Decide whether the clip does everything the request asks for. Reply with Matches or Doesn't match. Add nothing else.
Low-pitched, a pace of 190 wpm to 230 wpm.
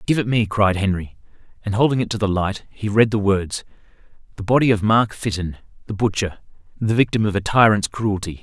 Matches